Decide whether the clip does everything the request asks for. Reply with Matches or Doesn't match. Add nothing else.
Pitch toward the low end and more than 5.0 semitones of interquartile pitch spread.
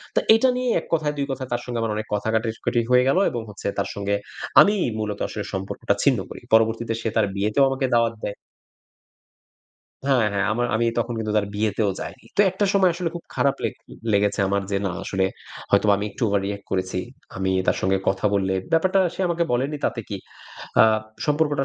Matches